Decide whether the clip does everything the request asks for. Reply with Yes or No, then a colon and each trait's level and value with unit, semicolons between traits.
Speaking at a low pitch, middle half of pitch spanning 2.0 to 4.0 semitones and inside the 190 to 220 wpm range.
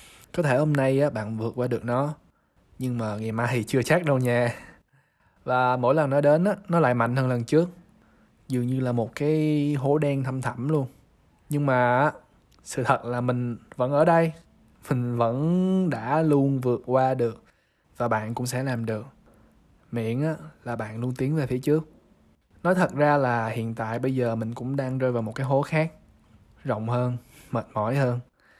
Yes: low, 125 Hz; average, 3.7 semitones; average, 195 wpm